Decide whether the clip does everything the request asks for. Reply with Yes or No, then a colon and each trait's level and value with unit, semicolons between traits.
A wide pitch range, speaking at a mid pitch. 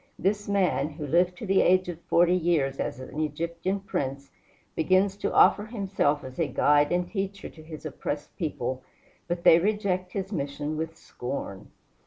No: average, 4.5 semitones; medium, 170 Hz